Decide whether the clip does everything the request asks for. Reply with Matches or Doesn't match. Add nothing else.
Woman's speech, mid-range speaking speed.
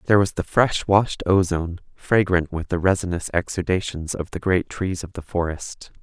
Doesn't match